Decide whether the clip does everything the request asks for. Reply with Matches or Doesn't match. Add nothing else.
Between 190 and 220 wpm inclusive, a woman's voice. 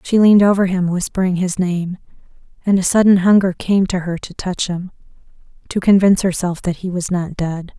Matches